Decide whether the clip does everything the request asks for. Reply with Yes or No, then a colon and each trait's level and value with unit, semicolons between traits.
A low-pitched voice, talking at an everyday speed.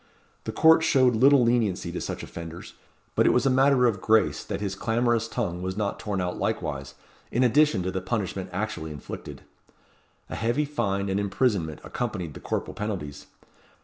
Yes: low, 105 Hz; average, 175 wpm